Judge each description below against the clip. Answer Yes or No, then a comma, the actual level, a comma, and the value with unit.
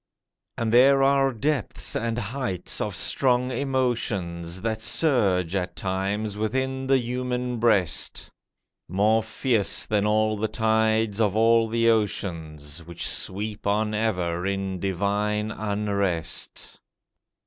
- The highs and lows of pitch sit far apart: No, average, 3.4 semitones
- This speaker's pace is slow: Yes, slow, 115 wpm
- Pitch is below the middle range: Yes, low, 110 Hz